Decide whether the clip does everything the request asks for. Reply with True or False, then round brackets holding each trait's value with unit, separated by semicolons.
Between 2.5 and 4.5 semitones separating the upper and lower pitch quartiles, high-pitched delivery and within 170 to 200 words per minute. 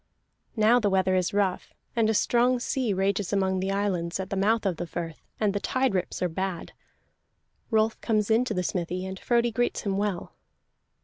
True (3.0 semitones; 200 Hz; 190 wpm)